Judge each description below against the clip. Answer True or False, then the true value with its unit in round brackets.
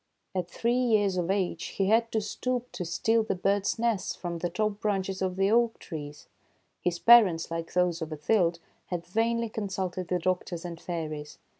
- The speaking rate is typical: True (180 wpm)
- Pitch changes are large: False (4.1 semitones)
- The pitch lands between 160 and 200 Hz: True (190 Hz)